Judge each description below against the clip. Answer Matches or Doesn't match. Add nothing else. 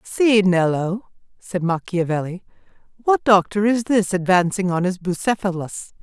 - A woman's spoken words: Matches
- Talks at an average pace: Doesn't match